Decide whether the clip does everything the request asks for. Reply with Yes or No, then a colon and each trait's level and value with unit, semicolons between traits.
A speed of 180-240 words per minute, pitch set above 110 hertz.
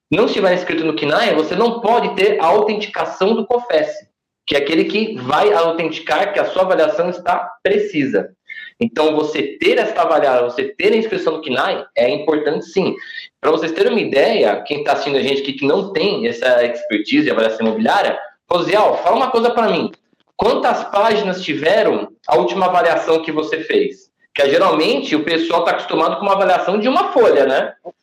Yes: fast, 185 wpm; high, 190 Hz